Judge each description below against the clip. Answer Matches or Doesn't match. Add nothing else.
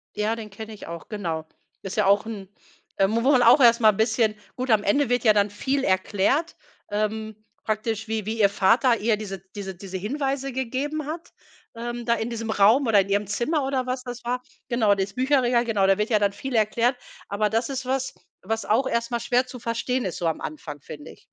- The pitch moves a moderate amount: Matches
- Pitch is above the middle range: Matches